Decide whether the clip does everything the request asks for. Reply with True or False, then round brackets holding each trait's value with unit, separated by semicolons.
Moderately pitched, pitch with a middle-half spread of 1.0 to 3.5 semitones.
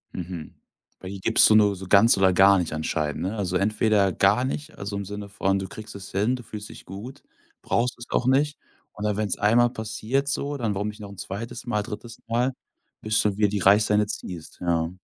False (105 Hz; 2.9 semitones)